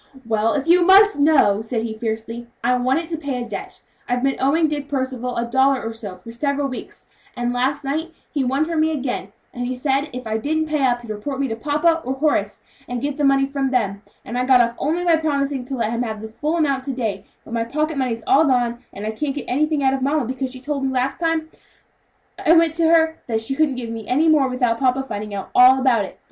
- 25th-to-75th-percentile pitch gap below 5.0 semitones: Yes, average, 3.9 semitones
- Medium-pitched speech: No, very high, 265 Hz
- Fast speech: Yes, fast, 255 wpm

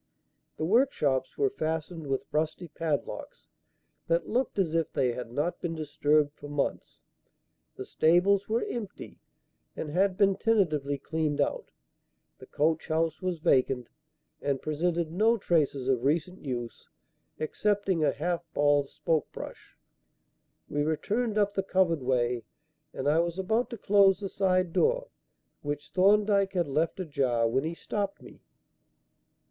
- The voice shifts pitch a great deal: No, average, 4.9 semitones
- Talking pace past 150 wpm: No, average, 140 wpm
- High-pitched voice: No, medium, 165 Hz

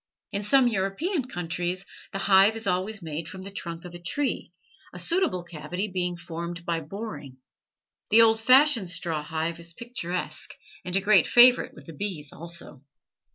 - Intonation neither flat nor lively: Yes, average, 4.4 semitones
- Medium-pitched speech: Yes, medium, 180 Hz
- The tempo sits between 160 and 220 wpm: Yes, average, 165 wpm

